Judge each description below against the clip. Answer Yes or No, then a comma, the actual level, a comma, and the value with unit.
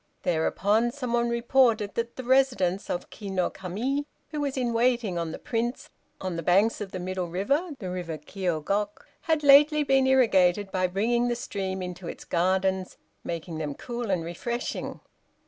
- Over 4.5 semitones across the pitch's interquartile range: Yes, average, 5.0 semitones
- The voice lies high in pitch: Yes, high, 205 Hz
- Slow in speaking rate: No, average, 170 wpm